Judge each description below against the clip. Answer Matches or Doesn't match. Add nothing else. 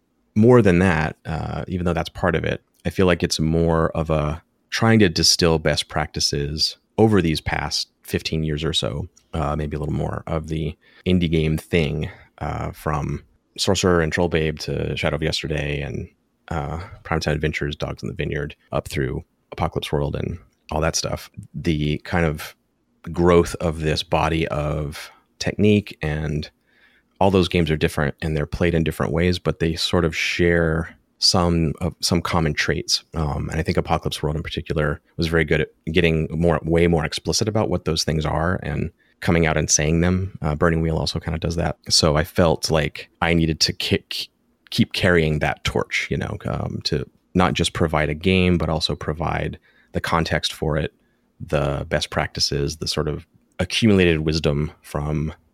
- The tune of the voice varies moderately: Doesn't match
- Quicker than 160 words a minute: Matches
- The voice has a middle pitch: Doesn't match